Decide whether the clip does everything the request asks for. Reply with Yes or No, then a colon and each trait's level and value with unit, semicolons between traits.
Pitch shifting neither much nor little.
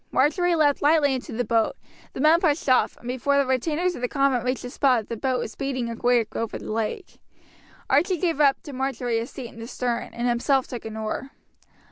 Yes: average, 3.3 semitones